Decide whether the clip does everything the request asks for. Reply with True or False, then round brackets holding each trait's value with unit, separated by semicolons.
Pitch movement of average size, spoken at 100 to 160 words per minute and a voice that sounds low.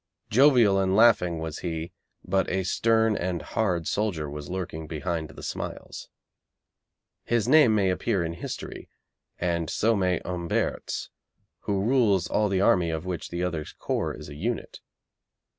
True (4.3 semitones; 150 wpm; 90 Hz)